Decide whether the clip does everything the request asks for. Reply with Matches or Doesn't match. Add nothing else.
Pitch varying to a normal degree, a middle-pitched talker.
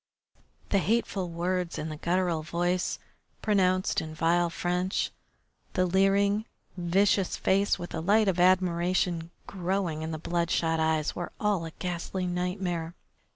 Doesn't match